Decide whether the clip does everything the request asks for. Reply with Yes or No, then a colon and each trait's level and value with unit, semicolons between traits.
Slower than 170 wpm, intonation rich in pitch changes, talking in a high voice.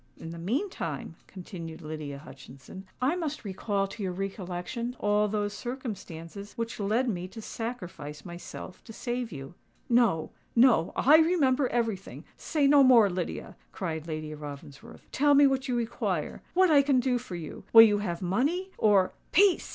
Yes: average, 155 wpm; wide, 6.6 semitones; high, 210 Hz